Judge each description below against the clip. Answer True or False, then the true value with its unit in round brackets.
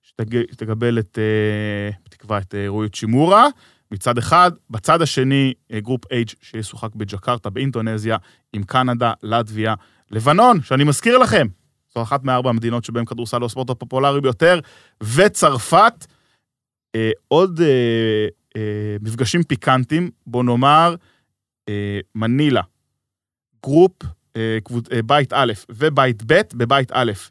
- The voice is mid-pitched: False (120 Hz)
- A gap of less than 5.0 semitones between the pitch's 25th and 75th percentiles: True (3.5 semitones)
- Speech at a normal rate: True (120 wpm)